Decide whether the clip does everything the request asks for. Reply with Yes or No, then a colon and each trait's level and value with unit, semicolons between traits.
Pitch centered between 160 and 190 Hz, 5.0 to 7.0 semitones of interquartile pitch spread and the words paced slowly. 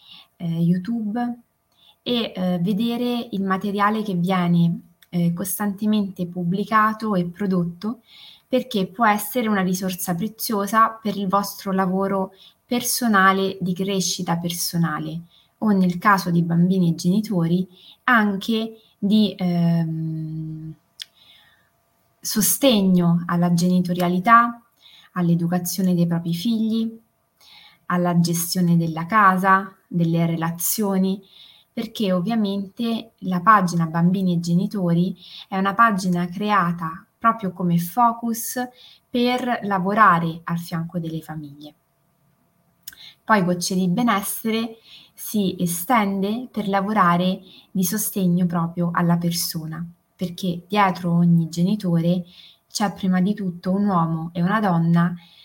No: medium, 185 Hz; average, 3.5 semitones; slow, 105 wpm